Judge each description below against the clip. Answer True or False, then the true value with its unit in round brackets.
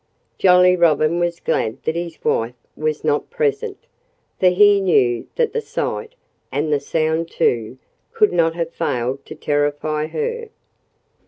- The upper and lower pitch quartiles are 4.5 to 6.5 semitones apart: True (5.1 semitones)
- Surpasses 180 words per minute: False (145 wpm)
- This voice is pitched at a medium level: True (165 Hz)